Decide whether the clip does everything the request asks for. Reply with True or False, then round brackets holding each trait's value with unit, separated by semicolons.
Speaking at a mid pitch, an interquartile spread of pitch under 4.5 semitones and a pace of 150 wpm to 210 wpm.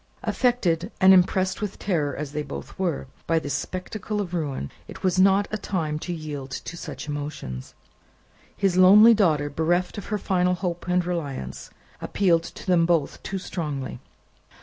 True (175 Hz; 3.9 semitones; 165 wpm)